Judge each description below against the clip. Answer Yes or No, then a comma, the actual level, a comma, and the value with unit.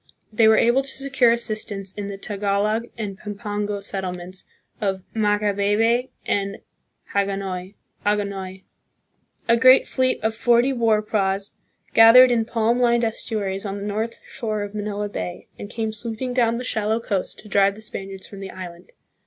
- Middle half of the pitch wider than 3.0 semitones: No, narrow, 2.5 semitones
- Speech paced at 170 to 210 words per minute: No, average, 155 wpm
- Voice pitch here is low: No, high, 210 Hz